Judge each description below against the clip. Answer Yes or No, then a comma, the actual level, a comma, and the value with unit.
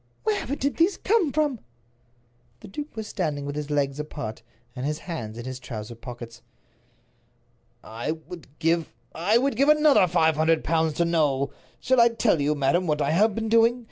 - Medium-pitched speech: Yes, medium, 165 Hz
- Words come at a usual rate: Yes, average, 175 wpm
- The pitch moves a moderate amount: No, wide, 8.2 semitones